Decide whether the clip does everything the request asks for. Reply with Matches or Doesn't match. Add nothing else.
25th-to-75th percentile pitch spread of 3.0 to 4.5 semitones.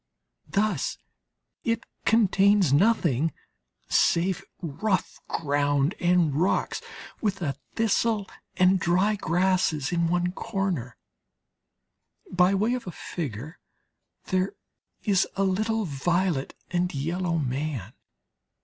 Matches